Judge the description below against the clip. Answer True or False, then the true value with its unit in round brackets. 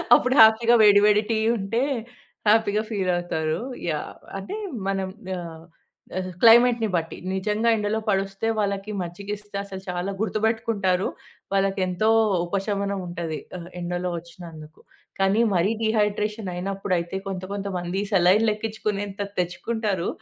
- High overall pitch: True (195 Hz)